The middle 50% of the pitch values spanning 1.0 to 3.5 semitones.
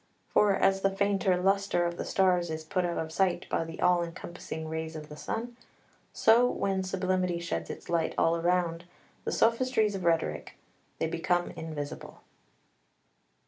Yes: average, 2.9 semitones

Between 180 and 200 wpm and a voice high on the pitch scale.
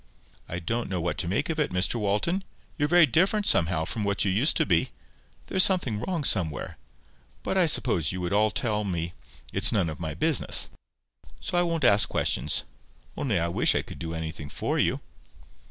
No: average, 195 wpm; low, 105 Hz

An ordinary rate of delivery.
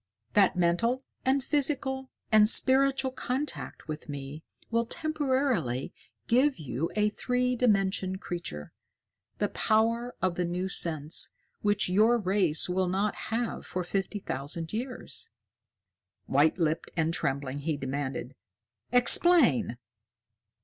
No: slow, 115 wpm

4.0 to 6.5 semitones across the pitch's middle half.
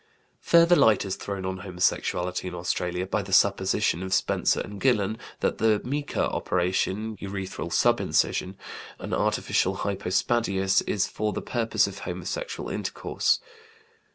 No: average, 2.7 semitones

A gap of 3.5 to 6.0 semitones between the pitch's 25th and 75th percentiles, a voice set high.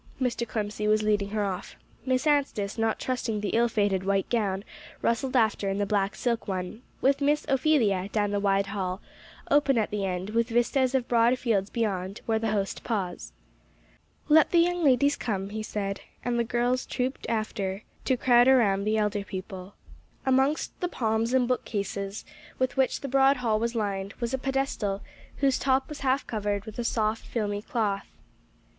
Yes: average, 4.1 semitones; high, 220 Hz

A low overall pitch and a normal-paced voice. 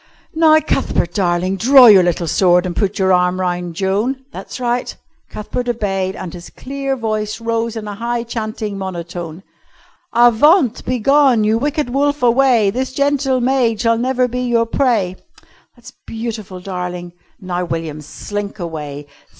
No: high, 220 Hz; average, 150 wpm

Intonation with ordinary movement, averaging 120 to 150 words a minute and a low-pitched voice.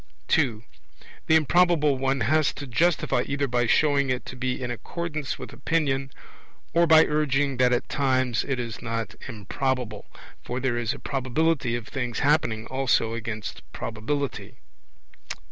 Yes: average, 3.5 semitones; average, 145 wpm; low, 130 Hz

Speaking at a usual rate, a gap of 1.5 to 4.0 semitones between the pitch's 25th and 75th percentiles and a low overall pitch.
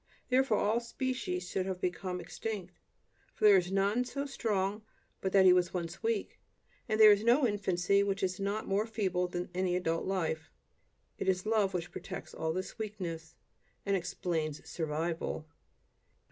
No: average, 160 wpm; average, 3.2 semitones; high, 190 Hz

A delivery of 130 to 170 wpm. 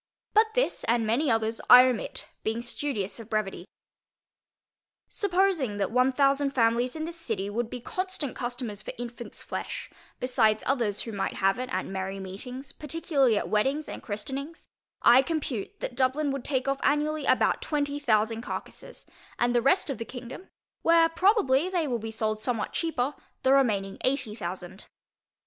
Yes: average, 165 wpm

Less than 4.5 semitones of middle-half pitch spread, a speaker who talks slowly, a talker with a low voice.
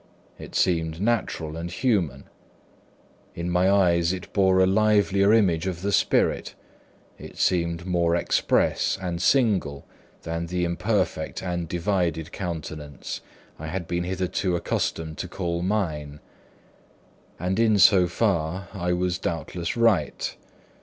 Yes: narrow, 2.4 semitones; slow, 125 wpm; very low, 90 Hz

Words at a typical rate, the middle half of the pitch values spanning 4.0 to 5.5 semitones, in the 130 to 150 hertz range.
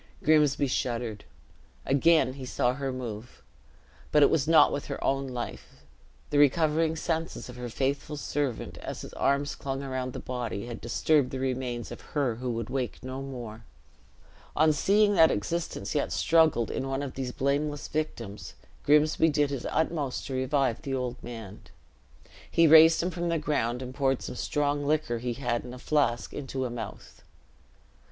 No: average, 170 wpm; average, 3.4 semitones; low, 135 Hz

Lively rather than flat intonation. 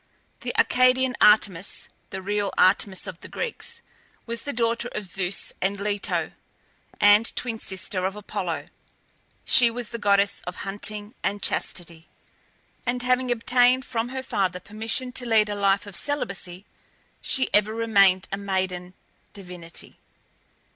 No: average, 3.6 semitones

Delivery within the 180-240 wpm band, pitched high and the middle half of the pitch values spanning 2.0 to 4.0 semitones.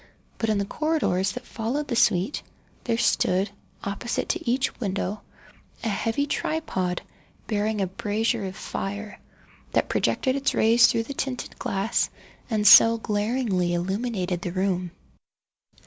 No: slow, 135 wpm; high, 215 Hz; average, 3.7 semitones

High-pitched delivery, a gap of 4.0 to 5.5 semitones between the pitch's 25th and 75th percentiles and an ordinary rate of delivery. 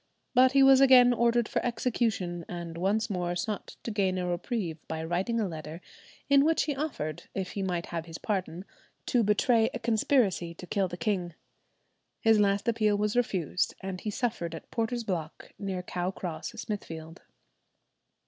Yes: high, 200 Hz; average, 5.0 semitones; average, 170 wpm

